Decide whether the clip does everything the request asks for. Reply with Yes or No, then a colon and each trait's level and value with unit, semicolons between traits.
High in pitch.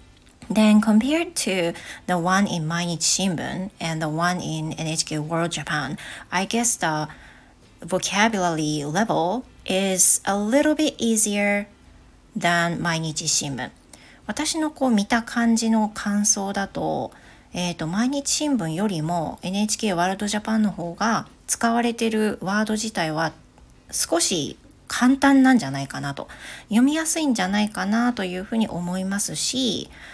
Yes: high, 200 Hz